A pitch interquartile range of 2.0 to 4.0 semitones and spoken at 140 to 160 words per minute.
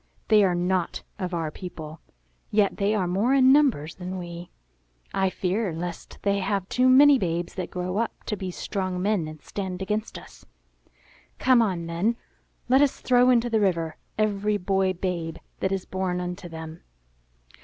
No: average, 3.3 semitones; average, 170 wpm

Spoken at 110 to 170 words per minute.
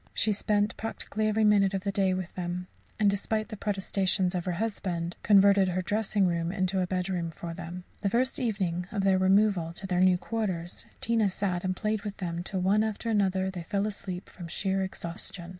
No: average, 200 wpm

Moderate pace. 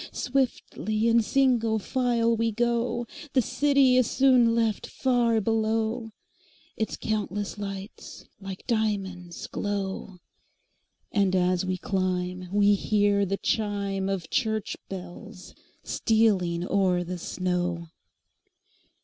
No: slow, 95 wpm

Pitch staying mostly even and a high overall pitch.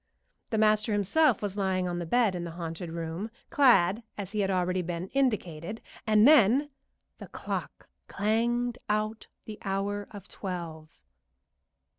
No: average, 3.7 semitones; high, 200 Hz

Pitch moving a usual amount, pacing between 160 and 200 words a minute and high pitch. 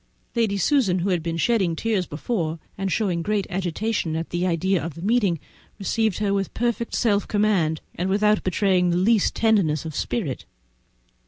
Yes: average, 3.9 semitones; average, 170 wpm; high, 195 Hz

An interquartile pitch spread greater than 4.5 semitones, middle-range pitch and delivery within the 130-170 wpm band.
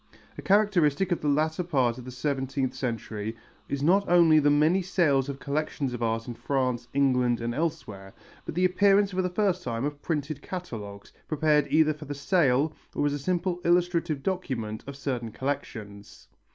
No: average, 5.3 semitones; medium, 145 Hz; average, 180 wpm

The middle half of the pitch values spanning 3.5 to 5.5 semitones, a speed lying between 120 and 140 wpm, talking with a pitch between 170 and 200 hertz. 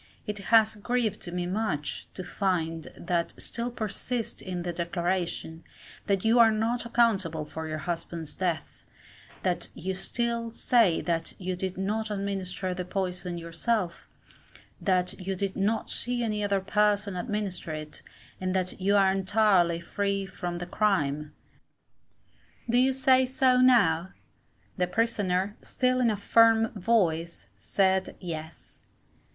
Yes: average, 4.1 semitones; slow, 135 wpm; high, 190 Hz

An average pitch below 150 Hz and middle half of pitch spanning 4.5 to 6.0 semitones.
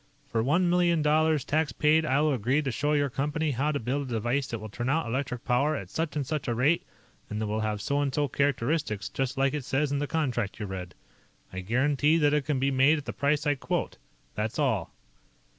No: medium, 140 Hz; average, 3.8 semitones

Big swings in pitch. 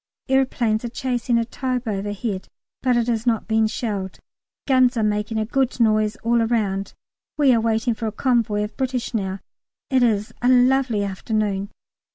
No: average, 2.8 semitones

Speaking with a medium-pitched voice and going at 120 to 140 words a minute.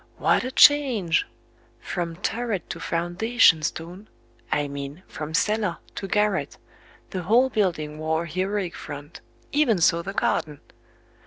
Yes: medium, 180 Hz; slow, 135 wpm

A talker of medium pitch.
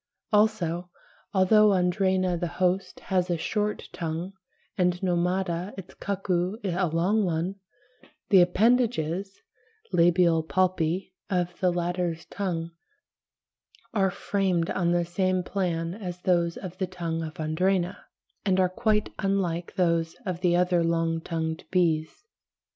Yes: medium, 180 Hz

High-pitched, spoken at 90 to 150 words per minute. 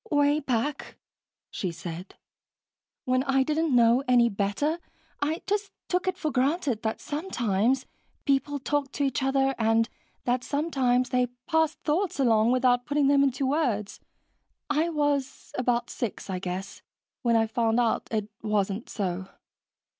Yes: very high, 255 Hz; average, 145 wpm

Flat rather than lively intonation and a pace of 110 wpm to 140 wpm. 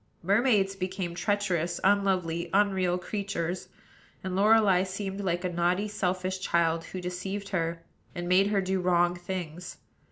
Yes: narrow, 2.1 semitones; slow, 135 wpm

